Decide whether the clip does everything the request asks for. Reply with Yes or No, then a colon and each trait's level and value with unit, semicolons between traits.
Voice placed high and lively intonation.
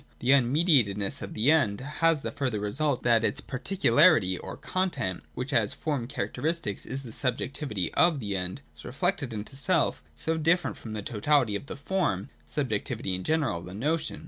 No: low, 130 Hz; wide, 7.0 semitones